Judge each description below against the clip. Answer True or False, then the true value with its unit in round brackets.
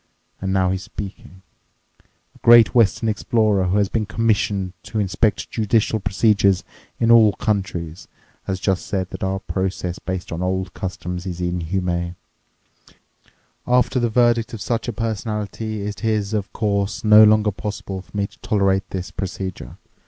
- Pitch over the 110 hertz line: False (100 Hz)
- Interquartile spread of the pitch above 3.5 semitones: False (2.6 semitones)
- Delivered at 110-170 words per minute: True (150 wpm)